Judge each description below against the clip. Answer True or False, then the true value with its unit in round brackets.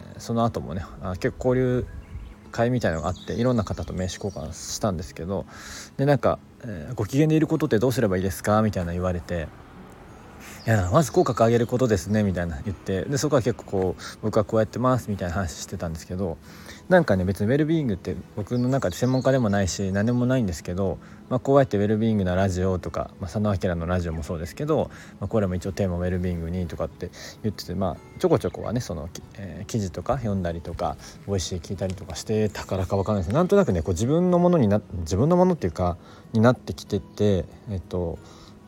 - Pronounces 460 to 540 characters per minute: True (475 characters per minute)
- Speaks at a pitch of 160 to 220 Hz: False (100 Hz)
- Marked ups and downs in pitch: False (4.4 semitones)